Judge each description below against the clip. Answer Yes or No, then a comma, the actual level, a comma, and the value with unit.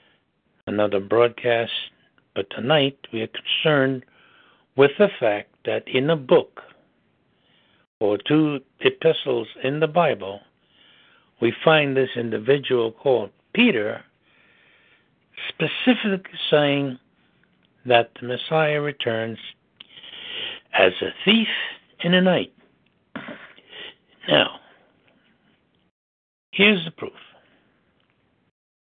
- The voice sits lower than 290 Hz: Yes, medium, 140 Hz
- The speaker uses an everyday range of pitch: No, wide, 6.8 semitones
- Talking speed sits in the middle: No, slow, 85 wpm